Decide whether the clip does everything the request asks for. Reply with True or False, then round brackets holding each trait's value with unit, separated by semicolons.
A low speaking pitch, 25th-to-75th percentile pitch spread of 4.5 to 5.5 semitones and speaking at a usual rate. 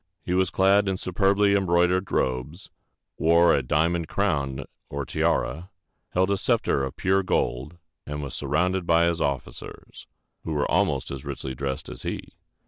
True (85 Hz; 5.0 semitones; 155 wpm)